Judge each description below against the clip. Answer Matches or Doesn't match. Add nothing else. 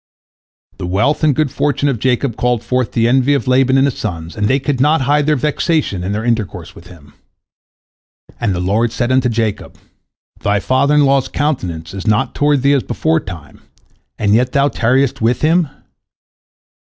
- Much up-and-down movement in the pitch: Doesn't match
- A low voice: Matches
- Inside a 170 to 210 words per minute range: Matches